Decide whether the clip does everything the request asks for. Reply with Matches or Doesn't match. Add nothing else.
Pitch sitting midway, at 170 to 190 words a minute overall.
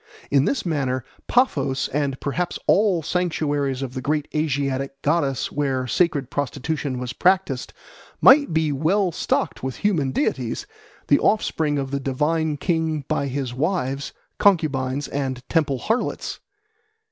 Doesn't match